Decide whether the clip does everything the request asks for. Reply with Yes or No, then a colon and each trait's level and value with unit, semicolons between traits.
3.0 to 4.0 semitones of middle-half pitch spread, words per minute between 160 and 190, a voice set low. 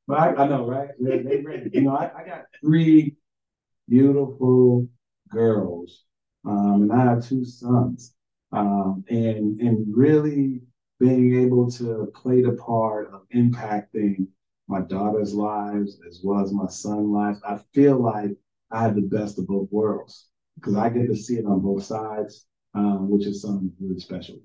Yes: average, 3.7 semitones; average, 165 wpm; low, 110 Hz